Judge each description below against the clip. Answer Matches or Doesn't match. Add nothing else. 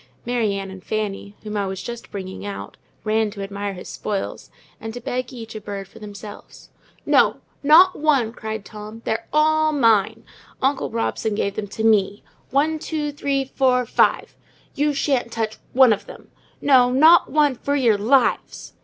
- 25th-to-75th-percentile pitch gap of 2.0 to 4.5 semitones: Doesn't match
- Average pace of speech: Matches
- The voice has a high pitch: Matches